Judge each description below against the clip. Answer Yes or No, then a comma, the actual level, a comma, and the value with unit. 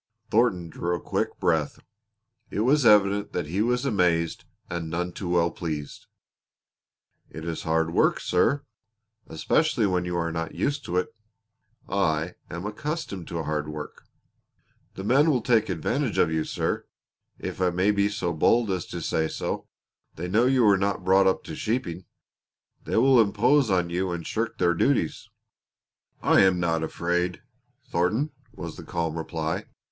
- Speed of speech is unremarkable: Yes, average, 160 wpm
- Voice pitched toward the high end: No, very low, 90 Hz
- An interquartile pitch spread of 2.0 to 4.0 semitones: No, average, 4.7 semitones